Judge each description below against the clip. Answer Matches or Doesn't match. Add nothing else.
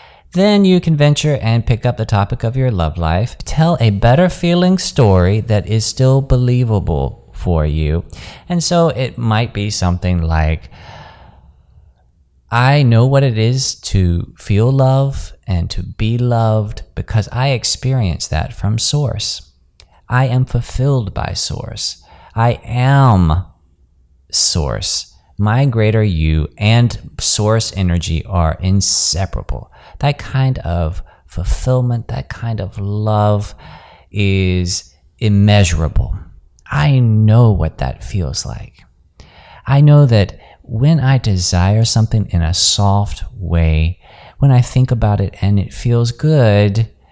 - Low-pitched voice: Matches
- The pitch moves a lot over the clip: Matches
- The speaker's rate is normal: Doesn't match